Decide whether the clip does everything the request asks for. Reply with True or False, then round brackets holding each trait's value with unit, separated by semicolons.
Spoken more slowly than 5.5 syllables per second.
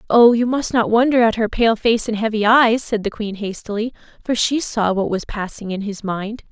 True (5.1 syllables/s)